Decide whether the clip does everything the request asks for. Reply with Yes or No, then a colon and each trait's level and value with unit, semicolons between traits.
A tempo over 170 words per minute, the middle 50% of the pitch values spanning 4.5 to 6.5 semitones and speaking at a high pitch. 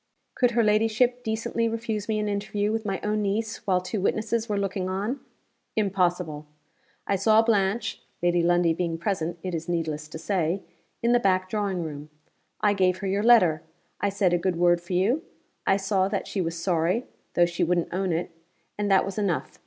No: average, 190 wpm; average, 3.4 semitones; high, 195 Hz